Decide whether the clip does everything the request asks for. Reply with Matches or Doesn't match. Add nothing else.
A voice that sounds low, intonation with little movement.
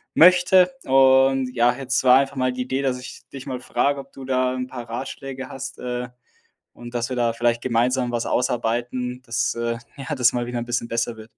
Matches